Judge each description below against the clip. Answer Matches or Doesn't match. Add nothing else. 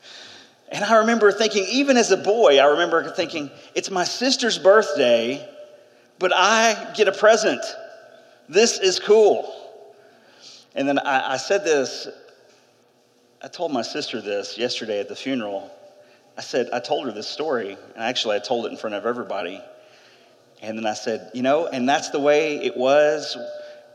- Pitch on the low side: Doesn't match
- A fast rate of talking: Doesn't match